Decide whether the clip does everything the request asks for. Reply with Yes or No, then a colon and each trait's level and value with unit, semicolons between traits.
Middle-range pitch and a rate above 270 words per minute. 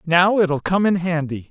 No: medium, 170 Hz; average, 200 wpm